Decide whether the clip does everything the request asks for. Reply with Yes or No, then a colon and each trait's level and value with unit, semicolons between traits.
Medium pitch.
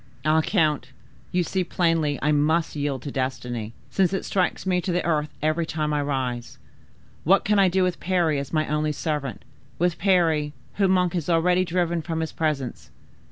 Yes: medium, 160 Hz